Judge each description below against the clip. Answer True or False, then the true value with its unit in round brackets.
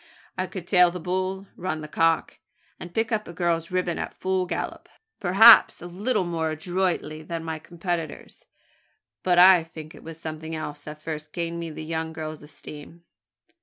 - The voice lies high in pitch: False (170 Hz)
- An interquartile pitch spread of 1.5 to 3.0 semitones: True (2.4 semitones)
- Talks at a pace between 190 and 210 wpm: False (175 wpm)